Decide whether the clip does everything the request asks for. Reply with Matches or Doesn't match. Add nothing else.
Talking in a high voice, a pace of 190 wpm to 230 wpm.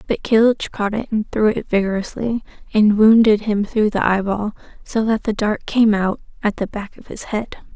Matches